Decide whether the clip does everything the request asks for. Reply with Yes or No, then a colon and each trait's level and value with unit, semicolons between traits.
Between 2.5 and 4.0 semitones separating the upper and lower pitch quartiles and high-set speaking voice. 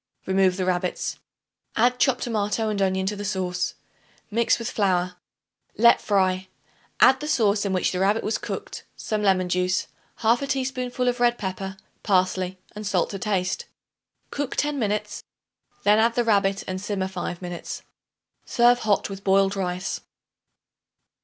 Yes: average, 3.6 semitones; high, 200 Hz